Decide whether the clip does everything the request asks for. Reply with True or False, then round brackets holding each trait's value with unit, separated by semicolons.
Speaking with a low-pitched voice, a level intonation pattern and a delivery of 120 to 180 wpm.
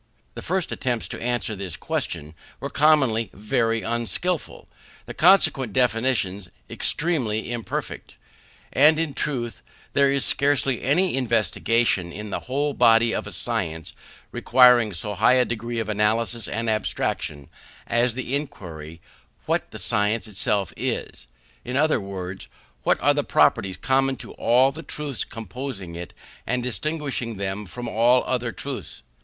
False (120 Hz; 4.2 semitones; 145 wpm)